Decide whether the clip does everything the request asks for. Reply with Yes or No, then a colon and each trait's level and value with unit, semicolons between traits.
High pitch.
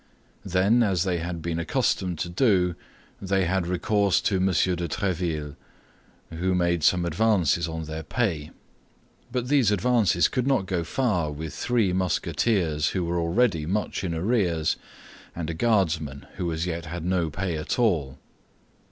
No: very low, 90 Hz